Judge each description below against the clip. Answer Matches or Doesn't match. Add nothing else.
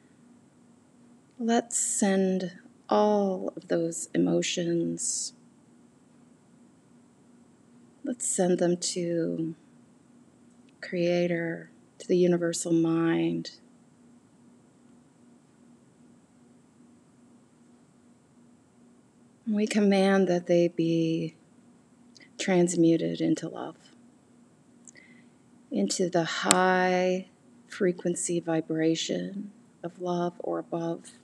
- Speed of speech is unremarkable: Doesn't match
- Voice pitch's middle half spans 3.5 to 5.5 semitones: Matches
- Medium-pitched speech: Matches